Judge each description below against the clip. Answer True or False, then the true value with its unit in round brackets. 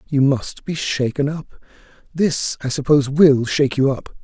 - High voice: False (140 Hz)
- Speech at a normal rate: True (170 wpm)